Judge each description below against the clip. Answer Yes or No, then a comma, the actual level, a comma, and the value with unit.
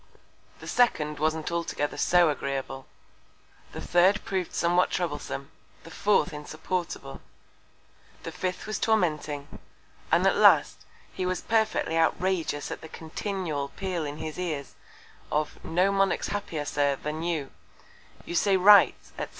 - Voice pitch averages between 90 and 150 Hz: No, medium, 165 Hz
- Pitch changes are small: No, average, 3.8 semitones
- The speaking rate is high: No, slow, 135 wpm